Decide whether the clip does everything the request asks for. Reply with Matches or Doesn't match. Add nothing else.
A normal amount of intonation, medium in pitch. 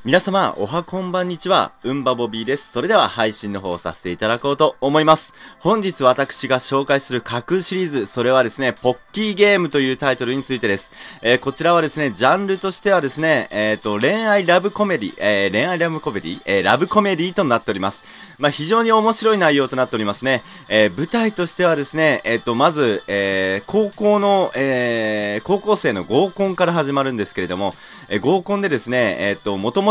Doesn't match